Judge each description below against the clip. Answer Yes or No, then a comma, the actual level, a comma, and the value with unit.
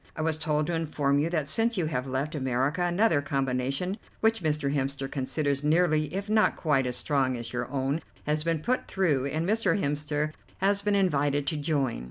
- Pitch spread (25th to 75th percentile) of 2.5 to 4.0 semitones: Yes, average, 3.7 semitones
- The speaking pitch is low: No, medium, 150 Hz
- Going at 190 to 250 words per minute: Yes, average, 195 wpm